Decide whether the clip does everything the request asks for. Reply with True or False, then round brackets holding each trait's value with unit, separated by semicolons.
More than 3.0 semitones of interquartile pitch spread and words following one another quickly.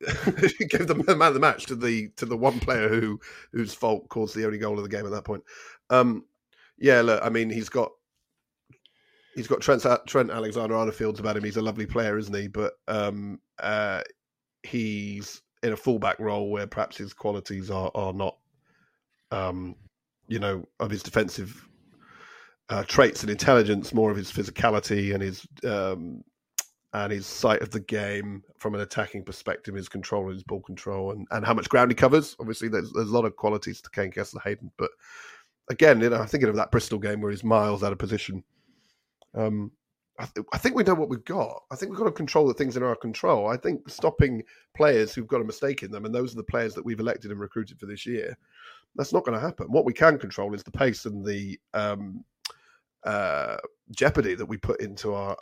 False (2.5 semitones; 210 wpm)